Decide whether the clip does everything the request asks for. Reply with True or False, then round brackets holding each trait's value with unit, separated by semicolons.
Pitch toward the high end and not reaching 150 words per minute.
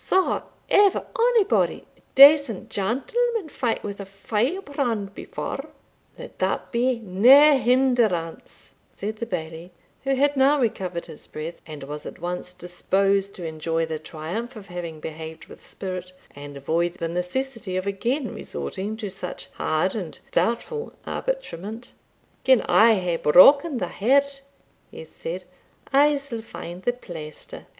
True (210 Hz; 140 wpm)